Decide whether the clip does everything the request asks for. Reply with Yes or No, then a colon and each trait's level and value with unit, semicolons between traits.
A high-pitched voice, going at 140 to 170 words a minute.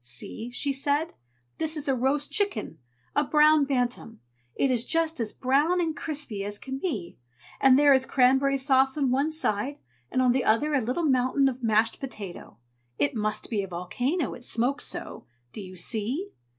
No: very high, 265 Hz; average, 185 wpm